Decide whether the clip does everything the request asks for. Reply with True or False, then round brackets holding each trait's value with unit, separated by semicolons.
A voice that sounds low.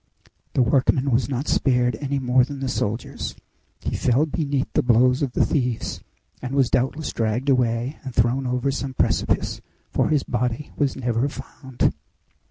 True (130 Hz)